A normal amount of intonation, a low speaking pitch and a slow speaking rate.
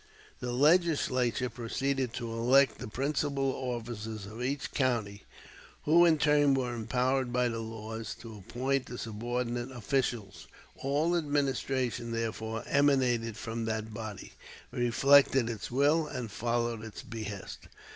Yes: average, 3.3 semitones; low, 120 Hz; slow, 125 wpm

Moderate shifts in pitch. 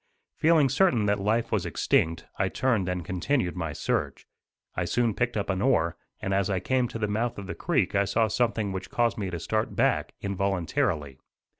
Yes: average, 4.2 semitones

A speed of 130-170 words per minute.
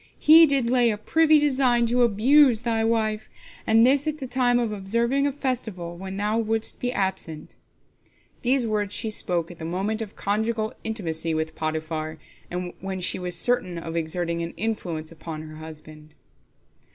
Yes: average, 165 wpm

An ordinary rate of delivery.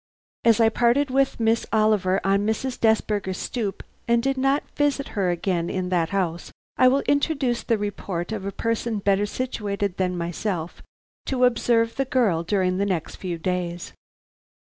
Yes: average, 165 wpm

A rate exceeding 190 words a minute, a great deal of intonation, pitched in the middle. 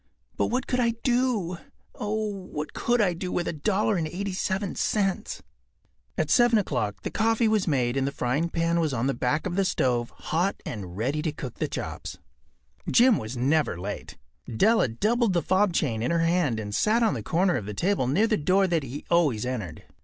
Yes: fast, 205 wpm; wide, 8.1 semitones; medium, 170 Hz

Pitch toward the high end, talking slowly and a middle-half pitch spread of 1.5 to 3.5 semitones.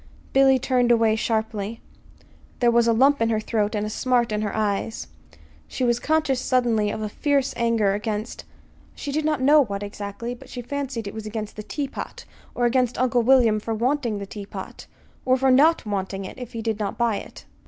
No: high, 230 Hz; average, 200 wpm; average, 3.2 semitones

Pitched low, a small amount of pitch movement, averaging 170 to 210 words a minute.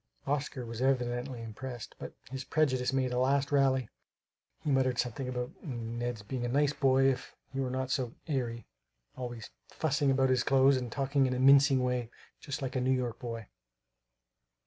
Yes: low, 130 Hz; narrow, 1.7 semitones; average, 175 wpm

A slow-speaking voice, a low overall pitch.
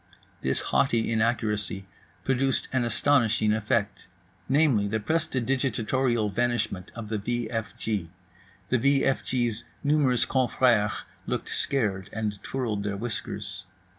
Yes: slow, 120 wpm; low, 115 Hz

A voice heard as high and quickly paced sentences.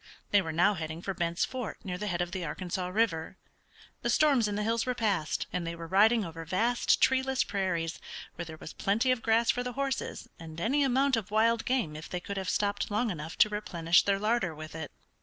Yes: high, 200 Hz; fast, 225 wpm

